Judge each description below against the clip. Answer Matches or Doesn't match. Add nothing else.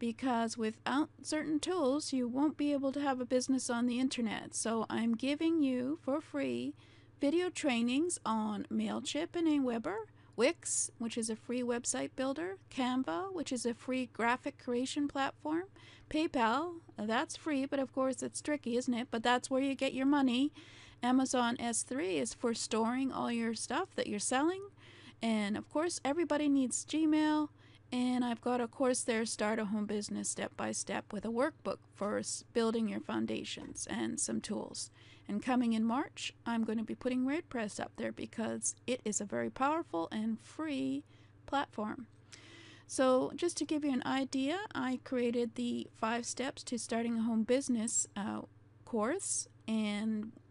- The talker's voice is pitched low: Doesn't match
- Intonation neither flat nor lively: Matches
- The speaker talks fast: Doesn't match